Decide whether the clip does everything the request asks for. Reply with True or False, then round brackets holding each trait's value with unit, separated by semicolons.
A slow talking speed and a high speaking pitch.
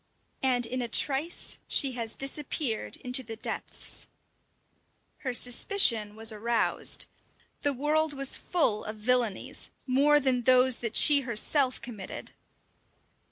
True (120 wpm; 250 Hz)